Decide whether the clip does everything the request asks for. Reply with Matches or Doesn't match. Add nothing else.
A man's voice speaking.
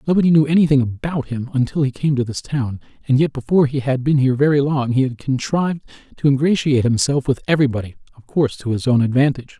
Matches